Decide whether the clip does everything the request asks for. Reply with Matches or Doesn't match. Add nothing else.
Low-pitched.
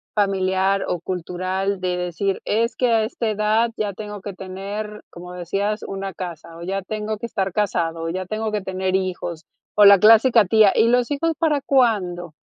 Doesn't match